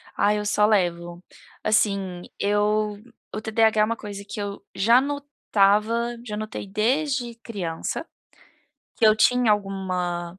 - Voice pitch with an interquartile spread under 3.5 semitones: Yes, narrow, 2.5 semitones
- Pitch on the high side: Yes, high, 210 Hz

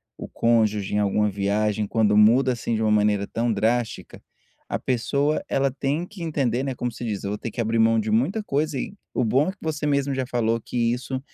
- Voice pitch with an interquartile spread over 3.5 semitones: Yes, average, 4.2 semitones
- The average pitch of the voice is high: No, low, 115 Hz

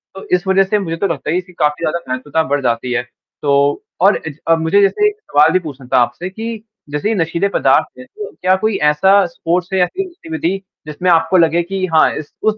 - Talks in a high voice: No, medium, 175 Hz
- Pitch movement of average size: Yes, average, 4.1 semitones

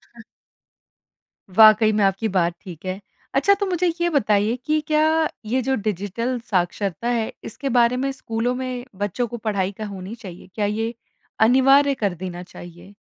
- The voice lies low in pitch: No, high, 220 Hz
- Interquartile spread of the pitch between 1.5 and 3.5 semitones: No, average, 4.8 semitones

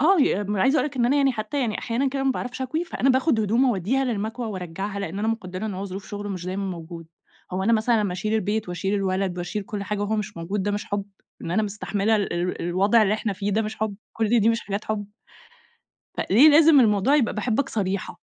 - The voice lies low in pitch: No, high, 210 Hz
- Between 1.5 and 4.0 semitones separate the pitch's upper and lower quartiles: Yes, average, 3.4 semitones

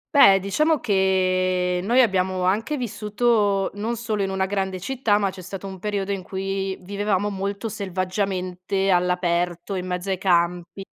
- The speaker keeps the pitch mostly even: Yes, narrow, 1.8 semitones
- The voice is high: Yes, high, 195 Hz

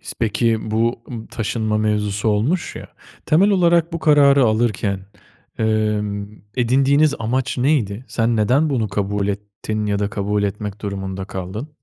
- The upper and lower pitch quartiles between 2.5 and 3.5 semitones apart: No, average, 4.2 semitones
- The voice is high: No, low, 110 Hz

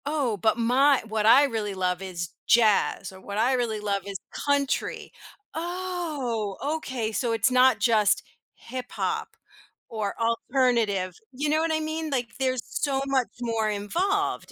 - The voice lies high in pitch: Yes, high, 240 Hz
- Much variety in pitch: No, average, 4.8 semitones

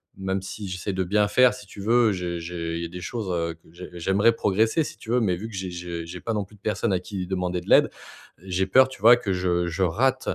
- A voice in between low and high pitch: No, very low, 95 Hz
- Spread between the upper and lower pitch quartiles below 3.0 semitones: No, average, 3.4 semitones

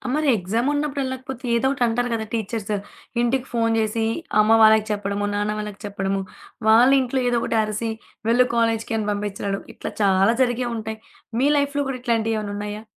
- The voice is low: No, high, 225 Hz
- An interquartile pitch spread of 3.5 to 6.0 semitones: No, average, 3.0 semitones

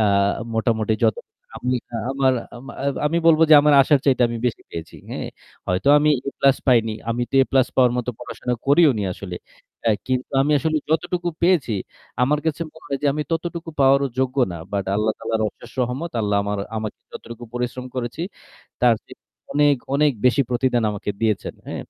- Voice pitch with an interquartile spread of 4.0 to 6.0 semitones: Yes, average, 4.4 semitones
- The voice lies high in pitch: No, low, 130 Hz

